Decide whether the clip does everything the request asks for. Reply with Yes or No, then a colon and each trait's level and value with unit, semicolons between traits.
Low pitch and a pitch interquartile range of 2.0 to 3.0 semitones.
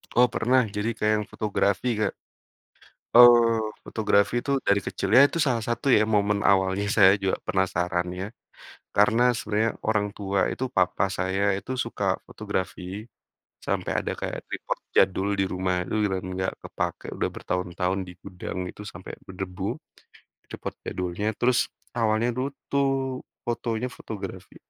No: low, 105 Hz; average, 3.4 semitones